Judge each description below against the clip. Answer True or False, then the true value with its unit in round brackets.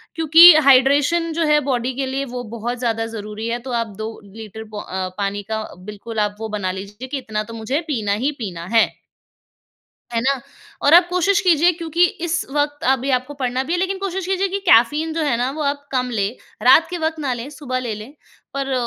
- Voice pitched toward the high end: True (260 Hz)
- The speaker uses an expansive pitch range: True (5.9 semitones)